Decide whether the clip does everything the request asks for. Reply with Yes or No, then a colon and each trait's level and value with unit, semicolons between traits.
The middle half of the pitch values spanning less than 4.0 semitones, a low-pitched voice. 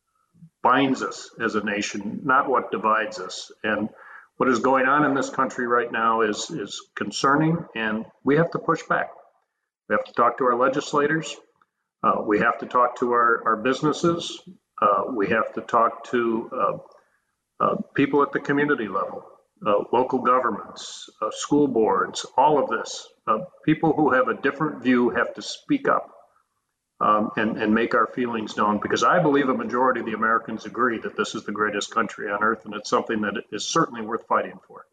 No: wide, 5.5 semitones; low, 130 Hz